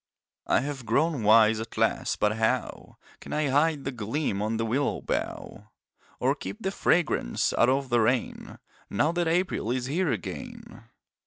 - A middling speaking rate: Yes, average, 165 wpm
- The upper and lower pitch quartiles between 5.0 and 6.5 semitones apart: Yes, wide, 5.4 semitones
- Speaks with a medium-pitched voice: No, low, 130 Hz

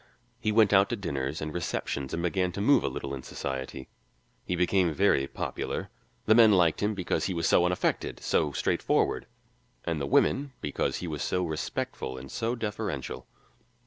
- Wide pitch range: Yes, wide, 6.5 semitones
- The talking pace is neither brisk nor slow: Yes, average, 175 wpm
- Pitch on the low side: Yes, very low, 90 Hz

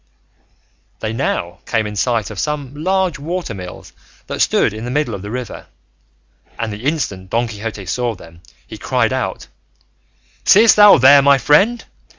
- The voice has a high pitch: No, low, 120 Hz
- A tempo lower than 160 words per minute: No, average, 165 wpm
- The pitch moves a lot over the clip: Yes, wide, 6.1 semitones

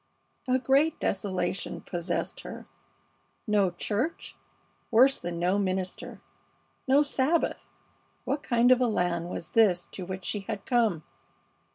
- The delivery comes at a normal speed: No, slow, 130 wpm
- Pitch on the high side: Yes, high, 205 Hz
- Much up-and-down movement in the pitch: Yes, wide, 6.0 semitones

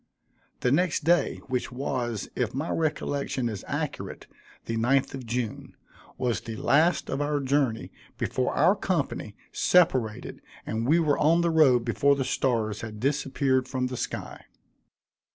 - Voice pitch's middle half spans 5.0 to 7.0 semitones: No, average, 3.7 semitones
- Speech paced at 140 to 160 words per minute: Yes, average, 150 wpm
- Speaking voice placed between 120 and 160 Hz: Yes, low, 135 Hz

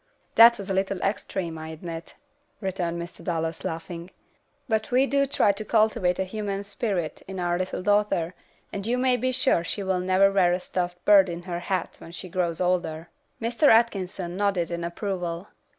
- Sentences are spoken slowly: No, average, 180 wpm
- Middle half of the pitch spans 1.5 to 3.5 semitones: Yes, average, 3.2 semitones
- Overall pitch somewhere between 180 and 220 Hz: Yes, medium, 185 Hz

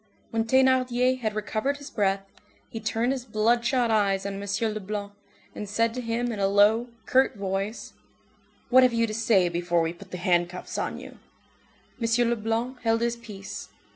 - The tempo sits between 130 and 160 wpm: No, average, 170 wpm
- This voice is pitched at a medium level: No, high, 225 Hz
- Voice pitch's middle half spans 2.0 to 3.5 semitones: Yes, average, 3.1 semitones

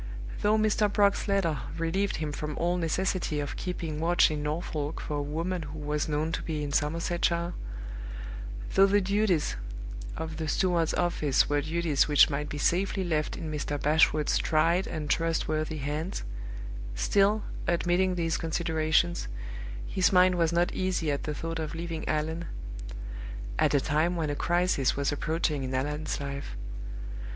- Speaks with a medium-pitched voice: Yes, medium, 160 Hz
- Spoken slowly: No, average, 155 wpm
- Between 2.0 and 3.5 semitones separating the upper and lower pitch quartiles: Yes, average, 2.8 semitones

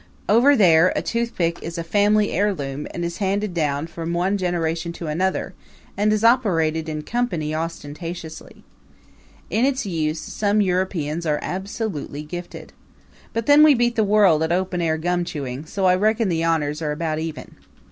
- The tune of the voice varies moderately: Yes, average, 4.4 semitones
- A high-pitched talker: No, medium, 175 Hz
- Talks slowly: No, average, 165 wpm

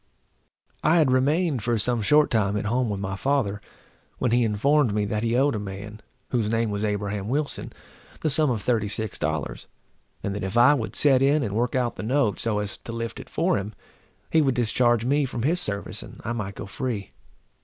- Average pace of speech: No, fast, 215 wpm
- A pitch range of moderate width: Yes, average, 4.2 semitones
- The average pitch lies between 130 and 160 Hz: No, low, 115 Hz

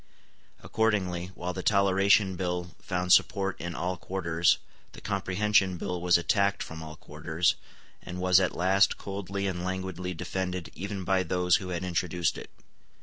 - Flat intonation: Yes, narrow, 1.7 semitones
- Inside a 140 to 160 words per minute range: Yes, average, 150 wpm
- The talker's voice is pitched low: Yes, very low, 90 Hz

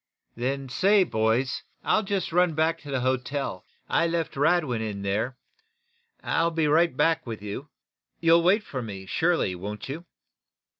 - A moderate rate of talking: Yes, average, 155 wpm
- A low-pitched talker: No, medium, 145 Hz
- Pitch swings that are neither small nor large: No, wide, 6.6 semitones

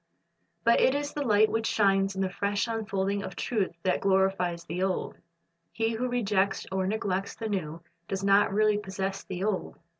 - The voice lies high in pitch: Yes, high, 200 Hz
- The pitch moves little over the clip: Yes, narrow, 2.2 semitones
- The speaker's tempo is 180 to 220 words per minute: Yes, average, 185 wpm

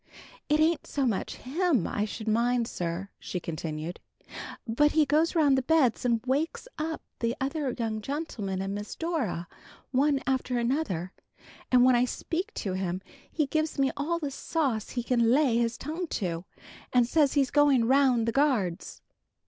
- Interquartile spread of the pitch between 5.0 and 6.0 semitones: Yes, average, 5.3 semitones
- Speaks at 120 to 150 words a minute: No, average, 170 wpm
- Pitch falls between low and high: No, very high, 255 Hz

